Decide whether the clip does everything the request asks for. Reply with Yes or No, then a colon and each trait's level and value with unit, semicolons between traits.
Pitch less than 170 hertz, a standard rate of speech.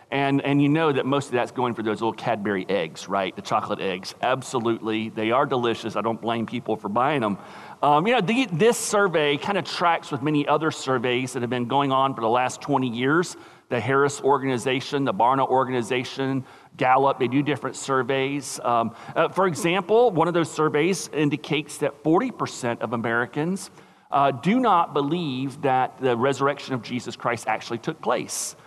Yes: low, 135 Hz; average, 185 wpm